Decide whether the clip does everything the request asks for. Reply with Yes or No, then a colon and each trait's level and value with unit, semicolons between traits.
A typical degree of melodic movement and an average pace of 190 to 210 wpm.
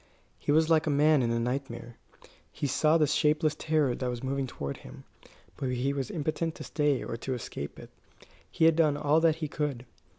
Yes: average, 3.5 semitones; fast, 205 wpm